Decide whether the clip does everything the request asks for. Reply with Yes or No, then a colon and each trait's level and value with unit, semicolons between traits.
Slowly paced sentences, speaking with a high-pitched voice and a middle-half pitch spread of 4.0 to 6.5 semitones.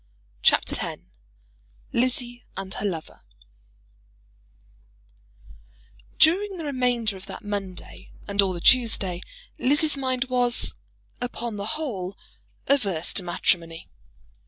Yes: slow, 105 wpm; high, 235 Hz; average, 5.1 semitones